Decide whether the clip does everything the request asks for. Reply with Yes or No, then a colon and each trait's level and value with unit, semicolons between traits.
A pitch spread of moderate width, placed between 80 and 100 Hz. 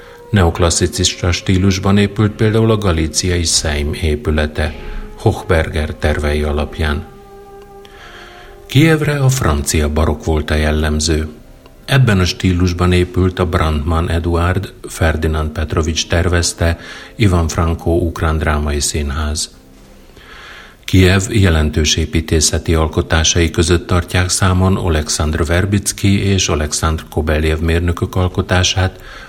Yes: average, 3.2 semitones; very low, 85 Hz